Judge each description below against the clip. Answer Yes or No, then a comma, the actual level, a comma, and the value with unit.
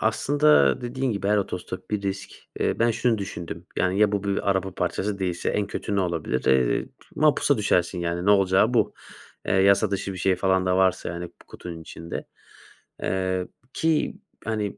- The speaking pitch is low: Yes, very low, 95 Hz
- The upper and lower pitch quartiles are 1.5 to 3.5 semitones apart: Yes, average, 2.8 semitones